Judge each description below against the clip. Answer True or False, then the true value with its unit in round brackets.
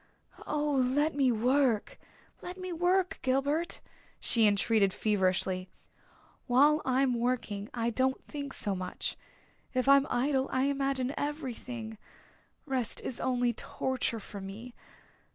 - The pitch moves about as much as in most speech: True (3.8 semitones)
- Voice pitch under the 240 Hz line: False (255 Hz)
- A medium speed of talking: False (120 wpm)